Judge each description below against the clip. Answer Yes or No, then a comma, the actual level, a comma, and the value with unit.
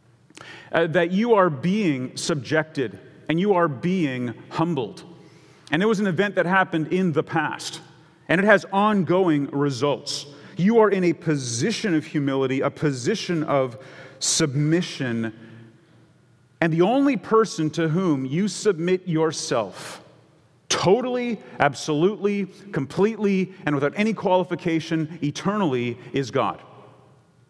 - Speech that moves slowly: Yes, slow, 120 wpm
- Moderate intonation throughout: Yes, average, 4.5 semitones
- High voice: No, medium, 165 Hz